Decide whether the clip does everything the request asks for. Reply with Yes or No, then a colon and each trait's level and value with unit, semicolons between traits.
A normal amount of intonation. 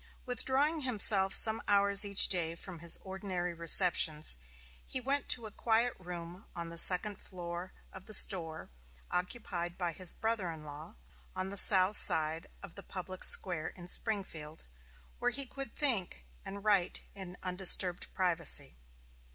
Yes: average, 3.2 semitones